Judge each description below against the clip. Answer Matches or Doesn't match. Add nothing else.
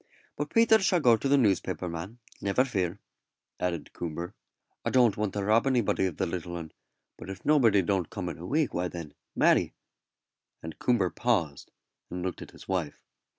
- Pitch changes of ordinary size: Doesn't match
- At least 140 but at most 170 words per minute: Doesn't match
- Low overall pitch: Matches